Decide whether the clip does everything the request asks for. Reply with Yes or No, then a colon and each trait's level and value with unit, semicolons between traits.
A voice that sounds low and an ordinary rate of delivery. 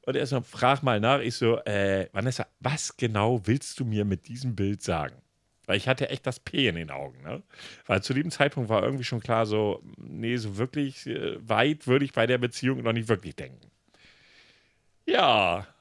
No: low, 120 Hz; fast, 195 wpm